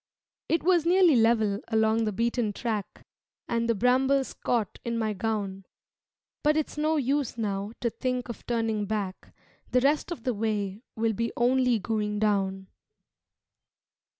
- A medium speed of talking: Yes, average, 150 wpm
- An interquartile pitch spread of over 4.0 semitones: No, average, 3.2 semitones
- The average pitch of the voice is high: Yes, high, 230 Hz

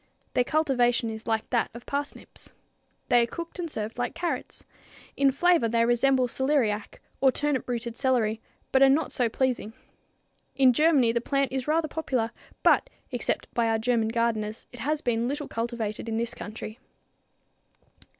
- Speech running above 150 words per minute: Yes, average, 160 wpm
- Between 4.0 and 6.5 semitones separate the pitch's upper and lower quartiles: No, average, 3.2 semitones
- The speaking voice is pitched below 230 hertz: No, high, 245 Hz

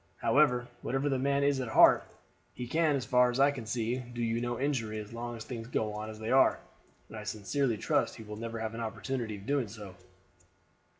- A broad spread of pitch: No, average, 3.3 semitones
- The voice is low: Yes, low, 120 Hz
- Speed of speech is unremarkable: No, fast, 220 wpm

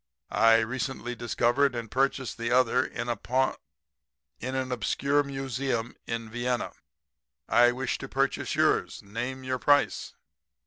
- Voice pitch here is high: No, low, 125 Hz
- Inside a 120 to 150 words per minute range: Yes, slow, 135 wpm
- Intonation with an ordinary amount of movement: No, narrow, 2.1 semitones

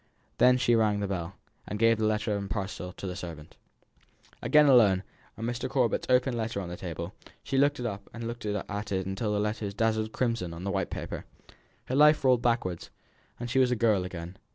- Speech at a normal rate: No, fast, 210 wpm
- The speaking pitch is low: Yes, low, 105 Hz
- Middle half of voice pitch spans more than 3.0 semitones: Yes, average, 3.7 semitones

